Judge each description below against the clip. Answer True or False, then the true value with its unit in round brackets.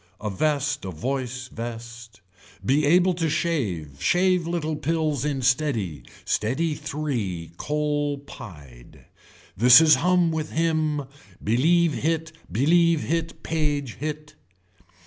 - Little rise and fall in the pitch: False (5.3 semitones)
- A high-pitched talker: False (145 Hz)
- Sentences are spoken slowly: True (115 wpm)